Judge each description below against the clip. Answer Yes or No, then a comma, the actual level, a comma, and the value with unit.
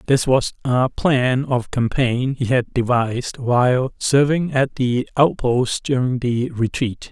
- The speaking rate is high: No, average, 145 wpm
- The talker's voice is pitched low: Yes, low, 125 Hz